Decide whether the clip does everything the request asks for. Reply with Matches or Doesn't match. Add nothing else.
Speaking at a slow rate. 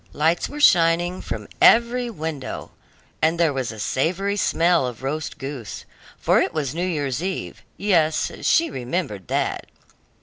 Doesn't match